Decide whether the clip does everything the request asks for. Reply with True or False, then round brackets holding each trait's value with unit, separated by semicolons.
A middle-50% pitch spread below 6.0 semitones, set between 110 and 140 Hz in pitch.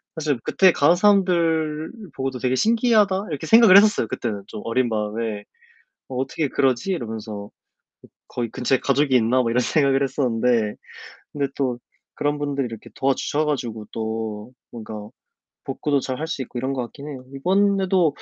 True (5.2 semitones; 135 Hz)